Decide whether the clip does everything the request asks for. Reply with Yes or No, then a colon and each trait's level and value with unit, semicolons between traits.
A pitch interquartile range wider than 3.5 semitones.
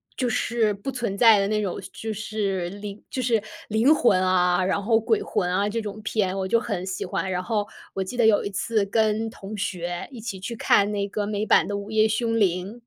No: narrow, 2.6 semitones